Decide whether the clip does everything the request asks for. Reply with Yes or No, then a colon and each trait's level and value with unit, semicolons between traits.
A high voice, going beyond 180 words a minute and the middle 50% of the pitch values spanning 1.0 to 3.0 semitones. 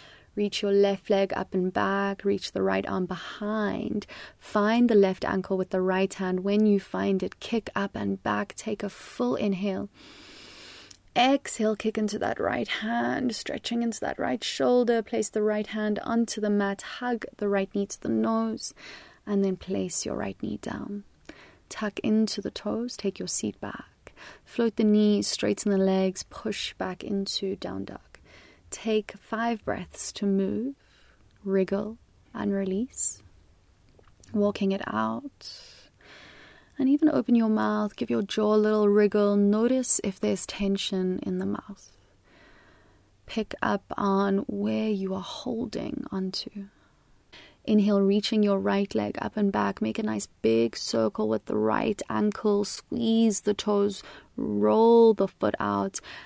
No: high, 200 Hz; average, 155 wpm; narrow, 2.4 semitones